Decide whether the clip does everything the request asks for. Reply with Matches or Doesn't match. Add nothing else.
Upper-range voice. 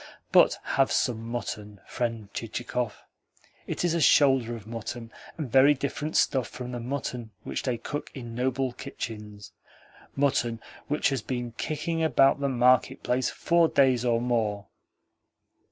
Doesn't match